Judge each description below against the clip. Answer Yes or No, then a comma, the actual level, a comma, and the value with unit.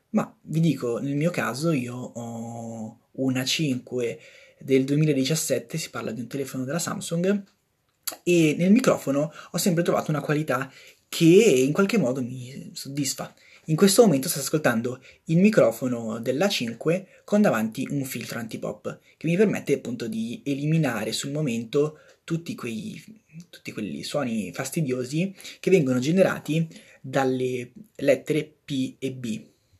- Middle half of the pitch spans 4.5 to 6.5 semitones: Yes, wide, 5.4 semitones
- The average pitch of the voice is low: No, medium, 145 Hz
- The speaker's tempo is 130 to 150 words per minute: Yes, average, 135 wpm